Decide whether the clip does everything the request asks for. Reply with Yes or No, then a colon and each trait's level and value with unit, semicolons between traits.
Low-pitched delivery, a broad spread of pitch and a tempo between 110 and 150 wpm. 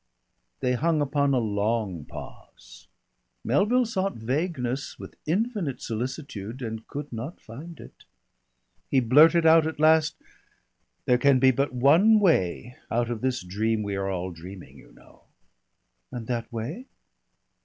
Yes: low, 130 Hz; wide, 6.1 semitones; average, 140 wpm